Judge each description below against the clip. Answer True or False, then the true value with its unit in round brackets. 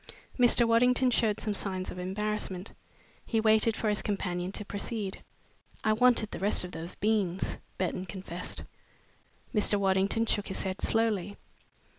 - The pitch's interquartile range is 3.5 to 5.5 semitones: False (2.8 semitones)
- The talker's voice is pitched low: False (205 Hz)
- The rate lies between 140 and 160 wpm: True (145 wpm)